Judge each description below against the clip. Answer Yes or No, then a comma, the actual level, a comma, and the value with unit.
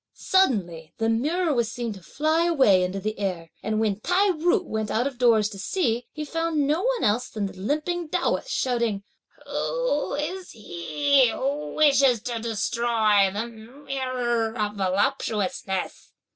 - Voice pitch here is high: Yes, high, 240 Hz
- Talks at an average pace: Yes, average, 155 wpm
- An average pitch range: No, wide, 6.0 semitones